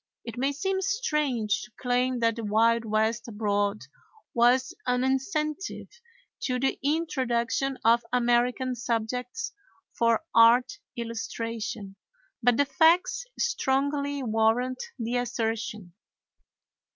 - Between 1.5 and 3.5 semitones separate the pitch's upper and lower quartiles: Yes, average, 3.0 semitones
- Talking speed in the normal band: No, slow, 105 wpm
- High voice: Yes, high, 245 Hz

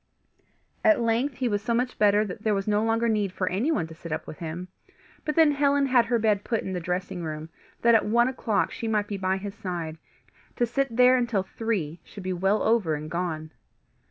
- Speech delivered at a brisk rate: Yes, fast, 220 wpm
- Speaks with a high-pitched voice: Yes, high, 210 Hz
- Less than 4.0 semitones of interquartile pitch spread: No, average, 4.6 semitones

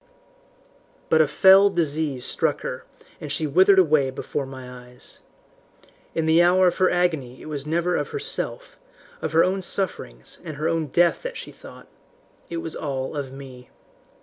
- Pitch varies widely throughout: No, average, 4.6 semitones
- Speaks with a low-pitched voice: No, medium, 160 Hz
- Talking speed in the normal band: Yes, average, 170 wpm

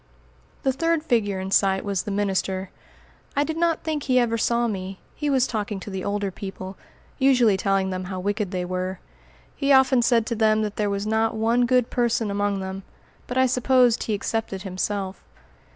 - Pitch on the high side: Yes, high, 210 Hz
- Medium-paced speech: Yes, average, 190 wpm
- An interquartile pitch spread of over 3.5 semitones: Yes, average, 4.2 semitones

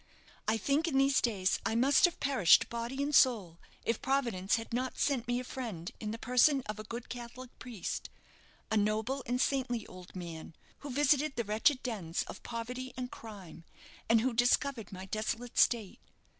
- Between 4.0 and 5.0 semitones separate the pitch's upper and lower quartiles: No, average, 3.5 semitones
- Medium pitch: No, high, 235 Hz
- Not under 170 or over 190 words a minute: Yes, average, 180 wpm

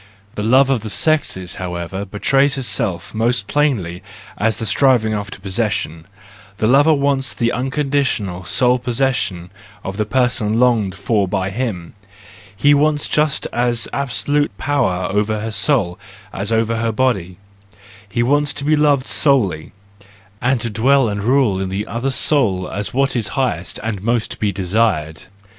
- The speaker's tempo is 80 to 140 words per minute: No, average, 155 wpm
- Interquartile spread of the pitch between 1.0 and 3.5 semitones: No, average, 5.3 semitones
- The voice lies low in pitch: Yes, low, 115 Hz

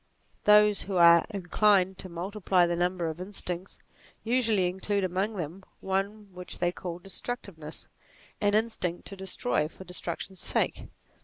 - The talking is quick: No, average, 145 wpm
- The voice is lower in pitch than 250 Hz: Yes, high, 190 Hz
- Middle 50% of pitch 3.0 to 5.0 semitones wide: No, narrow, 2.6 semitones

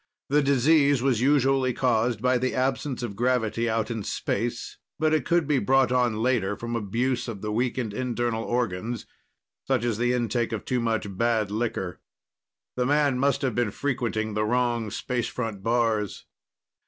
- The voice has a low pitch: Yes, low, 120 Hz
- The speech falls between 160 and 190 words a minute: Yes, average, 165 wpm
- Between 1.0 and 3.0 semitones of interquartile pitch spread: Yes, narrow, 2.4 semitones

